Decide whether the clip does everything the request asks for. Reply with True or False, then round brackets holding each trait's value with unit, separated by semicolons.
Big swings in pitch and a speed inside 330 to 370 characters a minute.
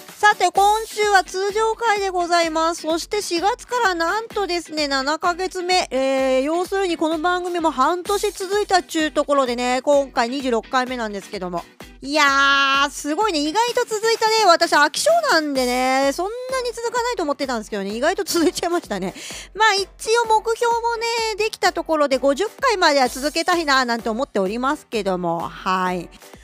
True (7.1 semitones; 355 characters per minute)